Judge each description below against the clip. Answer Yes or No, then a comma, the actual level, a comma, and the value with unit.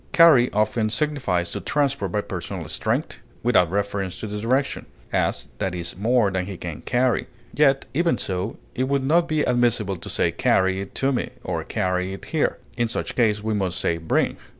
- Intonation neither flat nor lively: No, wide, 5.7 semitones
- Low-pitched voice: Yes, low, 110 Hz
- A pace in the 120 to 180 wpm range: No, average, 190 wpm